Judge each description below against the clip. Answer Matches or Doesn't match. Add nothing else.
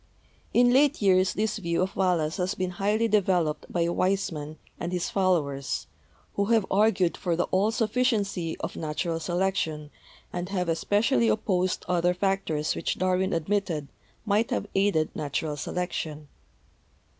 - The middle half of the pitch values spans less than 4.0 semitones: Matches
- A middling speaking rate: Matches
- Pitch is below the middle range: Doesn't match